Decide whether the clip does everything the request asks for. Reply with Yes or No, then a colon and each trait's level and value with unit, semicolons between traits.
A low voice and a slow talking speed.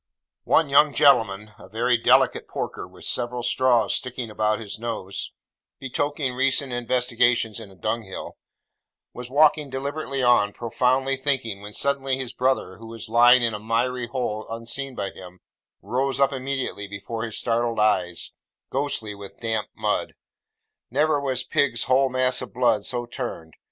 No: low, 120 Hz; average, 155 wpm